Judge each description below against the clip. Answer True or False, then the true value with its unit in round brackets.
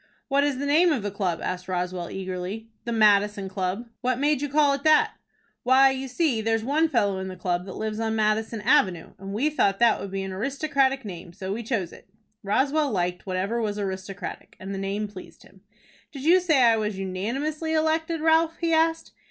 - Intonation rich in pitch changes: True (6.7 semitones)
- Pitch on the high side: True (220 Hz)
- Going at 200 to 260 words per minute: True (205 wpm)